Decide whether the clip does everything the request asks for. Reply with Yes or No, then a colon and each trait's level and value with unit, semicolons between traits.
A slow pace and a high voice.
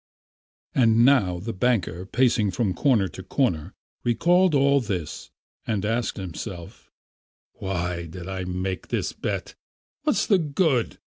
No: slow, 130 wpm; low, 105 Hz